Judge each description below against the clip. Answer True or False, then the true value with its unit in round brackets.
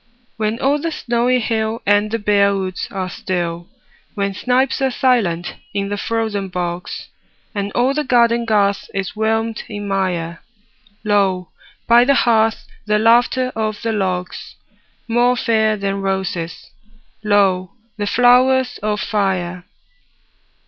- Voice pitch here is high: True (210 Hz)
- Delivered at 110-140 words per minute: True (135 wpm)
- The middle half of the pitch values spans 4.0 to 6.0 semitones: False (3.4 semitones)